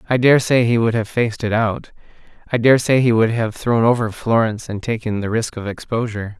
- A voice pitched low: Yes, low, 115 Hz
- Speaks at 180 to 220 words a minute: Yes, fast, 205 wpm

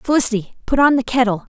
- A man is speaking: No, female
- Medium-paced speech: Yes, average, 195 wpm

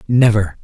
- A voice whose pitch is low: Yes, low, 110 Hz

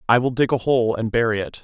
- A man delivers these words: Yes, male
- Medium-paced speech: No, fast, 295 wpm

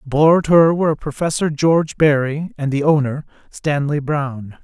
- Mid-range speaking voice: Yes, medium, 150 Hz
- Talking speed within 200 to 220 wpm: No, average, 155 wpm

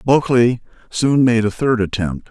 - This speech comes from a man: Yes, male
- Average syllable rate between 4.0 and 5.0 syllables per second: Yes, 4.8 syllables/s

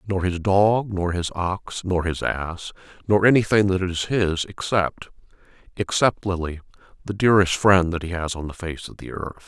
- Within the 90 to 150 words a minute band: No, average, 175 wpm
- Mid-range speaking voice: No, very low, 95 Hz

